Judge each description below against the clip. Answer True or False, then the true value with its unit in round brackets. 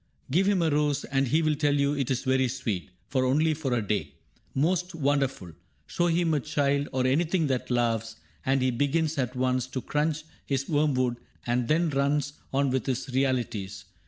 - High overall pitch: False (135 Hz)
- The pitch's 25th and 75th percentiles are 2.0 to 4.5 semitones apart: True (2.9 semitones)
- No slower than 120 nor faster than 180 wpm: False (195 wpm)